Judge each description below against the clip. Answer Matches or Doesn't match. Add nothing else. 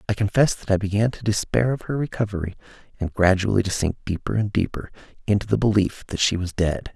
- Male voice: Matches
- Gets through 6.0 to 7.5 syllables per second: Matches